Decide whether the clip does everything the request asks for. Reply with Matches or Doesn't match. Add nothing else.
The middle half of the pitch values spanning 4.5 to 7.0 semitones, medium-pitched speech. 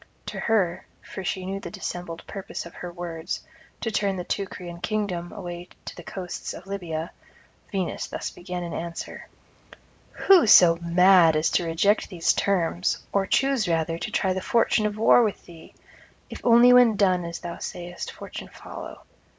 Doesn't match